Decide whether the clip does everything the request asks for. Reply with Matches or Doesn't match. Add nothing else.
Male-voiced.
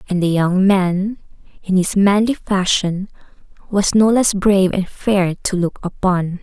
Doesn't match